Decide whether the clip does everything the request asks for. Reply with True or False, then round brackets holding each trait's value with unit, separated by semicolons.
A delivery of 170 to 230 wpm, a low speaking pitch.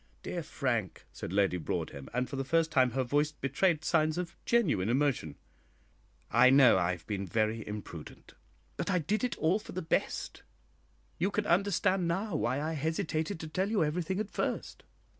False (180 wpm; 155 Hz)